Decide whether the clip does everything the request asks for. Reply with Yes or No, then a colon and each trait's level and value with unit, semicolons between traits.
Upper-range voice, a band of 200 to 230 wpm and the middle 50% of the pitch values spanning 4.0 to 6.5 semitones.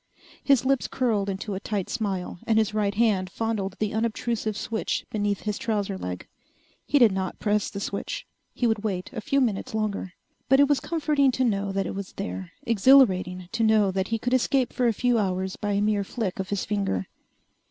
No: high, 210 Hz; fast, 205 wpm; average, 3.2 semitones